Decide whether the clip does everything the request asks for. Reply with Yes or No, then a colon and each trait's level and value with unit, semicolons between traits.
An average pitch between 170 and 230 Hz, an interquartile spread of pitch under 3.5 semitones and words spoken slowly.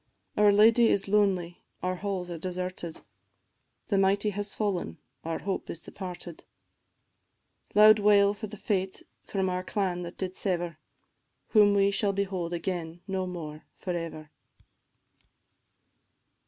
Yes: high, 190 Hz; narrow, 2.5 semitones; slow, 130 wpm